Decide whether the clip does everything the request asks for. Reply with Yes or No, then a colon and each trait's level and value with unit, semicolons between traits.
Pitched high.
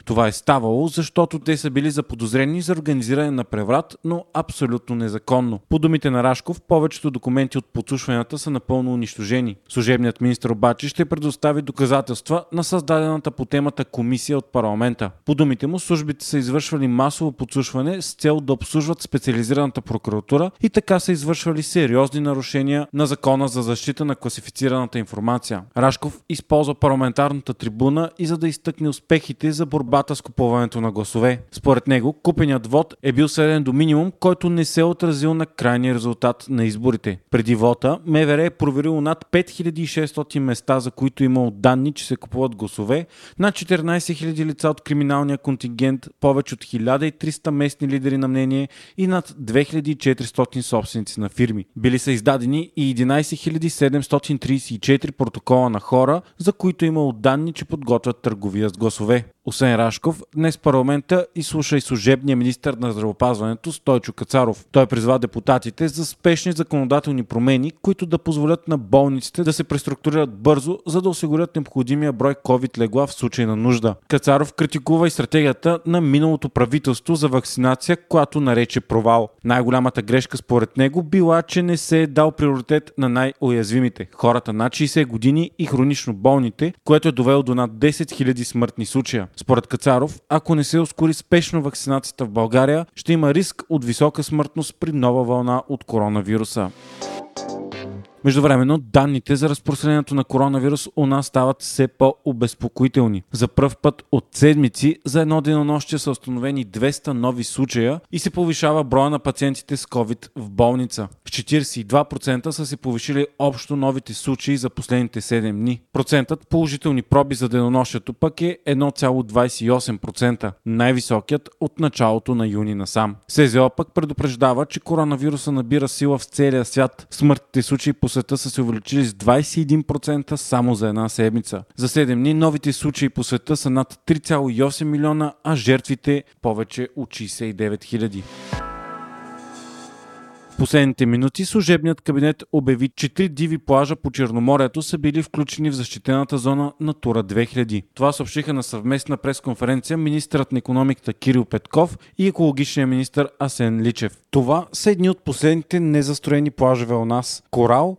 No: medium, 140 Hz